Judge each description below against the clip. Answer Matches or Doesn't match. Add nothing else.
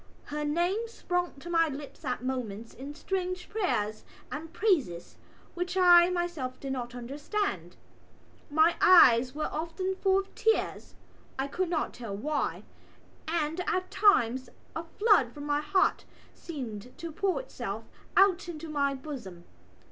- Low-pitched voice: Doesn't match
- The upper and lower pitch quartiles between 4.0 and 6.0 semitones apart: Matches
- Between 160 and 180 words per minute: Doesn't match